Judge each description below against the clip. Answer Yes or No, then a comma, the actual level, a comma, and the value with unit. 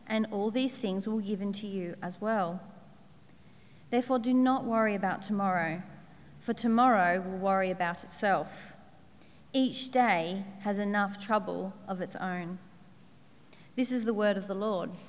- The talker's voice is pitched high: Yes, high, 200 Hz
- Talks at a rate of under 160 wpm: Yes, average, 150 wpm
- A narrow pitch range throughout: No, average, 3.6 semitones